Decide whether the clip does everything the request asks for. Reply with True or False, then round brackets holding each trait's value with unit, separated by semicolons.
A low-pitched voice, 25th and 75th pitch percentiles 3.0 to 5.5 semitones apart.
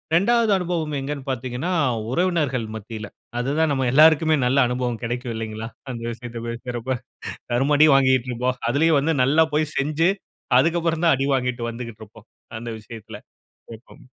True (130 Hz; 4.7 semitones)